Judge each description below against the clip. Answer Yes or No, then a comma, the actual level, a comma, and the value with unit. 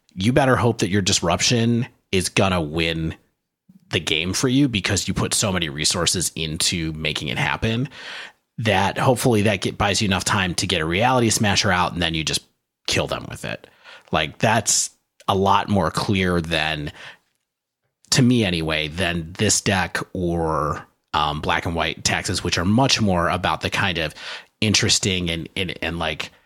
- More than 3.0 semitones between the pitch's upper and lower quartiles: Yes, average, 4.7 semitones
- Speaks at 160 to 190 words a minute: Yes, average, 175 wpm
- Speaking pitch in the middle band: No, very low, 95 Hz